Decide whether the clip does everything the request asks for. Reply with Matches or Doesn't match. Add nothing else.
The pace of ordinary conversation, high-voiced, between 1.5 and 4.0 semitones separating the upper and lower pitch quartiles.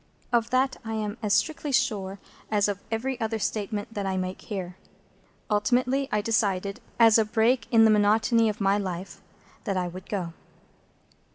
Matches